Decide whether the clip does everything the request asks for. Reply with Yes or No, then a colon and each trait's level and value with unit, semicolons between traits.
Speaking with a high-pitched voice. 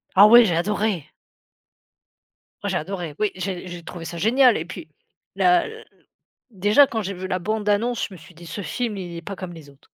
Yes: high, 195 Hz